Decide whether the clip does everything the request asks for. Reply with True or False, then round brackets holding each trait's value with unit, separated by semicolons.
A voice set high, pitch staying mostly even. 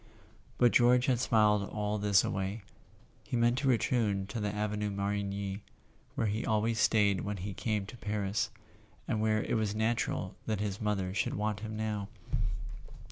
False (105 Hz; 1.6 semitones)